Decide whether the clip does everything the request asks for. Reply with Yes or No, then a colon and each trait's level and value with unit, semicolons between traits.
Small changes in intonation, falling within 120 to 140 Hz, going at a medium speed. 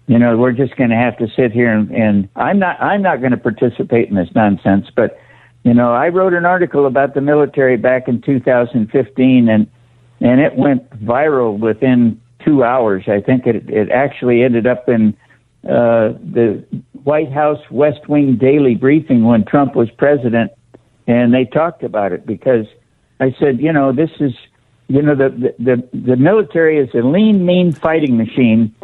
No: average, 3.4 semitones; low, 125 Hz; average, 185 wpm